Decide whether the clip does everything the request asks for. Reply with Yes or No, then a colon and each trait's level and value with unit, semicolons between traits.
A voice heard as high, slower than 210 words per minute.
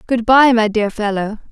Yes: high, 225 Hz; average, 200 wpm